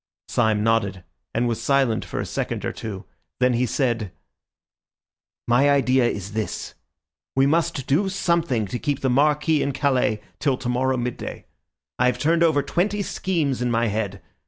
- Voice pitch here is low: Yes, low, 130 Hz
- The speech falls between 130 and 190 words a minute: Yes, average, 160 wpm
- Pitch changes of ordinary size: Yes, average, 4.2 semitones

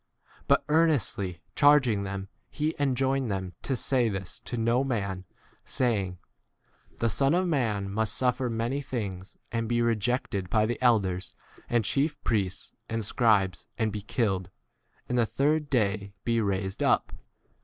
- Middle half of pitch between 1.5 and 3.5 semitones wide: No, average, 4.6 semitones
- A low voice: Yes, low, 115 Hz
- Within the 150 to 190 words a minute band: Yes, average, 155 wpm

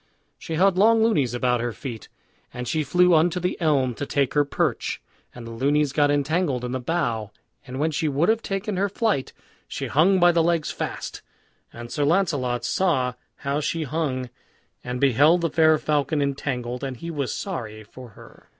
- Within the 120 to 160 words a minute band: No, average, 175 wpm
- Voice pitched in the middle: Yes, medium, 145 Hz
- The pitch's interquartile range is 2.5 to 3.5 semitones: No, average, 5.0 semitones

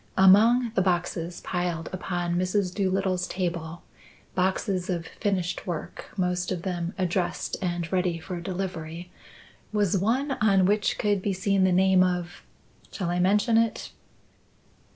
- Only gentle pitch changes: Yes, narrow, 1.8 semitones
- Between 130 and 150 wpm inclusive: Yes, slow, 135 wpm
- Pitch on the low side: No, medium, 185 Hz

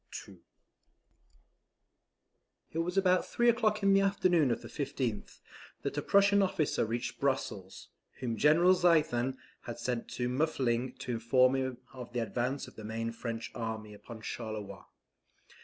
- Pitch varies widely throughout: Yes, wide, 6.4 semitones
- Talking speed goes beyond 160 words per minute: No, average, 145 wpm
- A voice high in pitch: No, low, 130 Hz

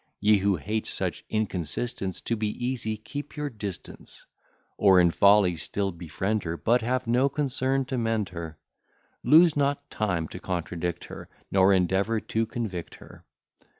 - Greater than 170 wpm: No, average, 150 wpm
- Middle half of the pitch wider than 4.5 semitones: Yes, average, 4.9 semitones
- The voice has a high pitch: No, low, 105 Hz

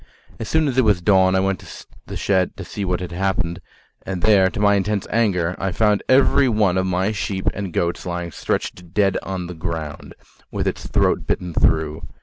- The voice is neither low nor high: No, very low, 95 Hz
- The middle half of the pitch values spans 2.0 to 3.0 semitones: Yes, average, 2.7 semitones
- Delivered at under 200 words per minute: No, fast, 205 wpm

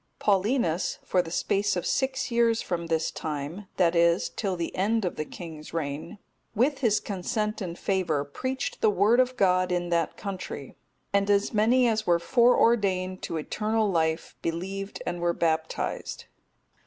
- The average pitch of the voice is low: No, medium, 185 Hz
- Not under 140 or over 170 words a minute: Yes, average, 160 wpm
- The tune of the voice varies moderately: Yes, average, 4.3 semitones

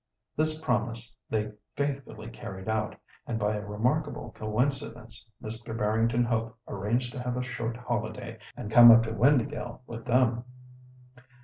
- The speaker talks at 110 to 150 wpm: Yes, average, 140 wpm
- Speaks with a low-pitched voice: Yes, low, 115 Hz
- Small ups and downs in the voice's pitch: Yes, narrow, 2.1 semitones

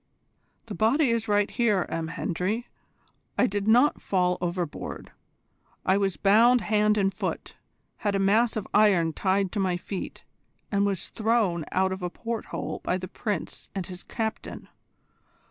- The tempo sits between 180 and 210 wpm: No, average, 165 wpm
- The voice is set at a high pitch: Yes, high, 200 Hz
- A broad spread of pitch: No, average, 3.0 semitones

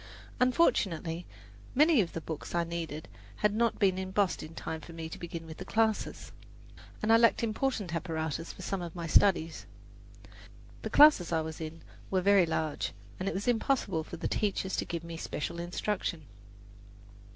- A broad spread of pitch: No, average, 4.3 semitones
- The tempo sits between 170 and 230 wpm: Yes, average, 175 wpm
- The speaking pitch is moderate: Yes, medium, 175 Hz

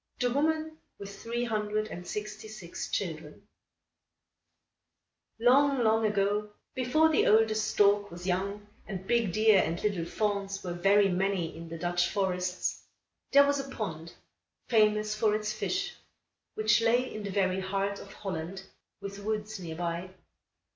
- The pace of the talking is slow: No, average, 145 wpm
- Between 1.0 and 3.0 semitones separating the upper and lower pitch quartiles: Yes, average, 2.7 semitones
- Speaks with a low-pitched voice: No, high, 205 Hz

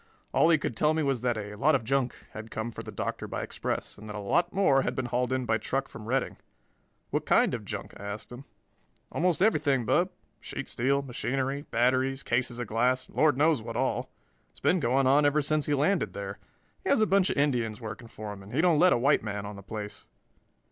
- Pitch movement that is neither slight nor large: Yes, average, 4.5 semitones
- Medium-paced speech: No, fast, 235 wpm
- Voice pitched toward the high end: No, low, 130 Hz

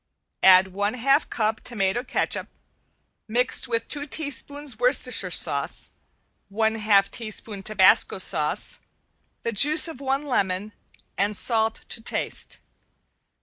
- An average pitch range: Yes, average, 4.4 semitones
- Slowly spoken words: Yes, slow, 115 wpm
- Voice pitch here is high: Yes, high, 225 Hz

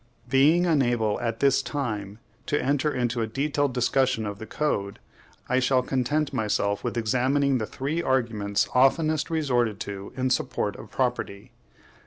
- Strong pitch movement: No, average, 4.1 semitones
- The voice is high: No, low, 125 Hz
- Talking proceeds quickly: No, average, 150 wpm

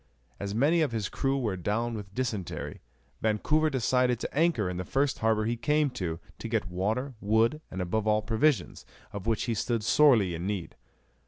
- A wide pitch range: No, average, 4.5 semitones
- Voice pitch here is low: Yes, low, 110 Hz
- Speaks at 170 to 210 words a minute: Yes, average, 185 wpm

